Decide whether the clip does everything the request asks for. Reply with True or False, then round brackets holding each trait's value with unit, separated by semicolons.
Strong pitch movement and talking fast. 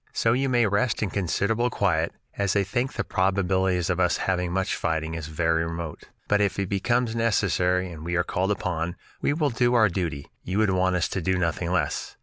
False (3.2 semitones; 210 wpm)